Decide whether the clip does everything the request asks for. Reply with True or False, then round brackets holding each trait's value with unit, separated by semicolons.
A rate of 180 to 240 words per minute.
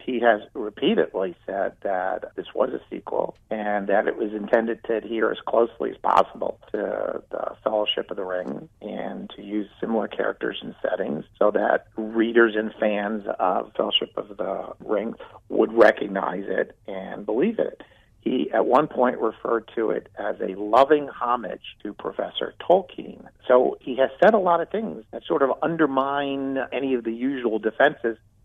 False (170 wpm)